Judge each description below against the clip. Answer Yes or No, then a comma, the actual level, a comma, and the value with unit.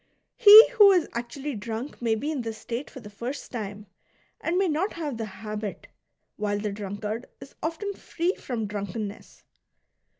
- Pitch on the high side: Yes, high, 235 Hz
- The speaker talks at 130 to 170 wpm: Yes, average, 165 wpm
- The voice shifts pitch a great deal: Yes, wide, 6.8 semitones